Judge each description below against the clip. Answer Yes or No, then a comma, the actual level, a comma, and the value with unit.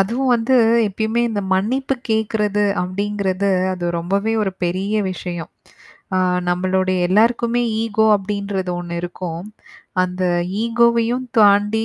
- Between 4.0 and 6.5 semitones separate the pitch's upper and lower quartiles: No, average, 3.3 semitones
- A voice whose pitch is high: Yes, high, 205 Hz